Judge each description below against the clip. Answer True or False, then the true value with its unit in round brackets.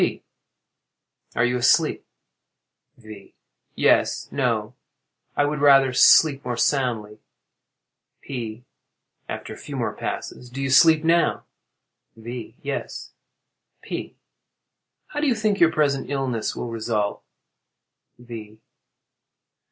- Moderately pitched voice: False (125 Hz)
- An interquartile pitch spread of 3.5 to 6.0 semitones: True (3.9 semitones)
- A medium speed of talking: False (105 wpm)